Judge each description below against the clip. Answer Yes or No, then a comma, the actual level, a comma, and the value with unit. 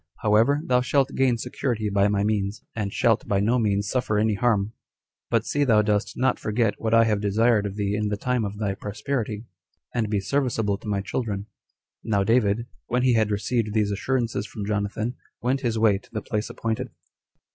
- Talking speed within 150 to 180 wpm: No, average, 195 wpm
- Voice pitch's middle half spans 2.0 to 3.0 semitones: Yes, narrow, 2.6 semitones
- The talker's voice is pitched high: No, low, 110 Hz